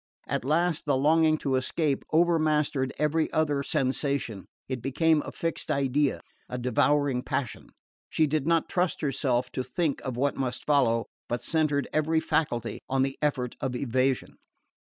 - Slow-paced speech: No, average, 155 wpm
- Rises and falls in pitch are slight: No, average, 3.2 semitones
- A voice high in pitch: No, medium, 140 Hz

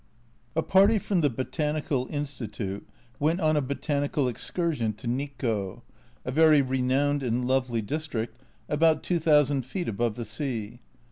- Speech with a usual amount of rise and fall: Yes, average, 4.4 semitones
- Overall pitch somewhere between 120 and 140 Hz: Yes, low, 135 Hz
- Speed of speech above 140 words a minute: No, slow, 135 wpm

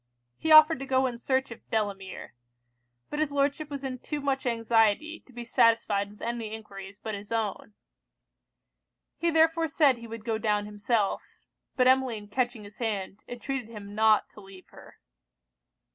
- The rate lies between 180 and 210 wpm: No, average, 165 wpm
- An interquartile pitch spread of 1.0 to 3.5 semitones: No, average, 4.3 semitones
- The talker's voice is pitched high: Yes, high, 230 Hz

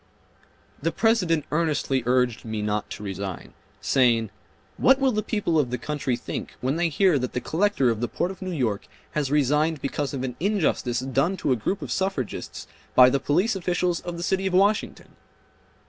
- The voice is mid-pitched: Yes, medium, 150 Hz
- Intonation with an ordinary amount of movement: No, wide, 6.4 semitones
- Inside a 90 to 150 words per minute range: No, average, 190 wpm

